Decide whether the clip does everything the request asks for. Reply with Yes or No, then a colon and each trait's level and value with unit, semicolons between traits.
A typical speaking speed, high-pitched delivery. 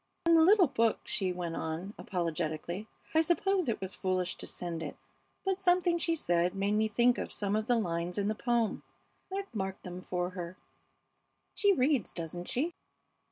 Yes: average, 180 wpm; high, 205 Hz